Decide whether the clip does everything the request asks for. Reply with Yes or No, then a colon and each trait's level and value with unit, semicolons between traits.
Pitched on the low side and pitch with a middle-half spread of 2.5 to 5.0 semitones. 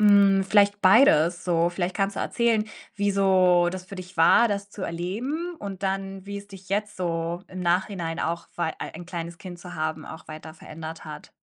No: medium, 185 Hz; average, 2.8 semitones